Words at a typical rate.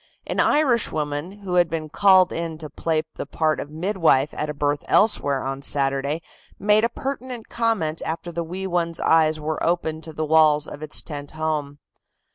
Yes: average, 185 wpm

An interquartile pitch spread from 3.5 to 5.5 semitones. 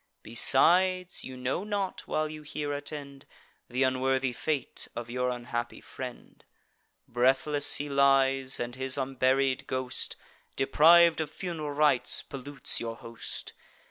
No: average, 2.7 semitones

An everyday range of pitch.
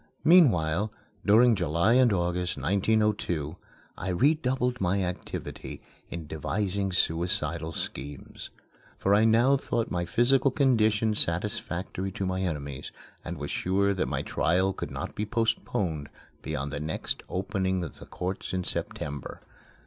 Yes: average, 4.6 semitones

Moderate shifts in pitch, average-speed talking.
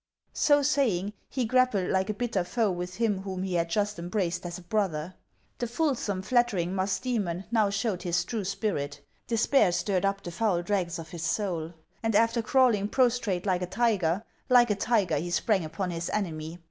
Yes: average, 4.4 semitones; average, 185 wpm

